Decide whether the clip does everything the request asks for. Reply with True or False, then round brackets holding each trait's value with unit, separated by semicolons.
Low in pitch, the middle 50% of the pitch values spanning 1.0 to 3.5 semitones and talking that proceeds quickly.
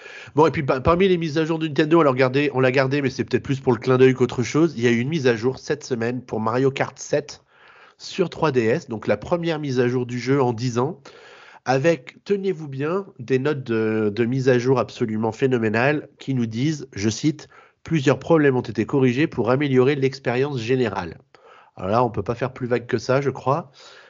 True (130 Hz; 2.9 semitones; 225 wpm)